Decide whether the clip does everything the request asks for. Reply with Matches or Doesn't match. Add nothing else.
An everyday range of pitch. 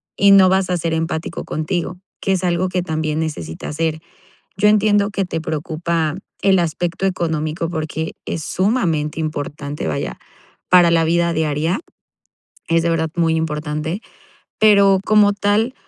Matches